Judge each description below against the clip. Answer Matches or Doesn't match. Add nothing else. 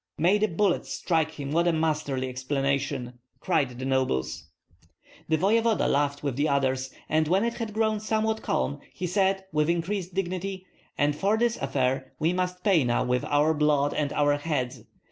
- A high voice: Doesn't match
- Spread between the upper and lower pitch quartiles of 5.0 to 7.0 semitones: Matches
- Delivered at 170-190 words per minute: Matches